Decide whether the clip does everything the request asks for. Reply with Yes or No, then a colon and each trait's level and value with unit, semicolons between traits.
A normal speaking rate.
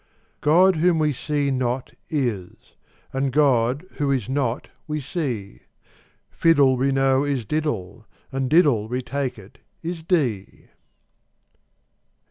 No: slow, 120 wpm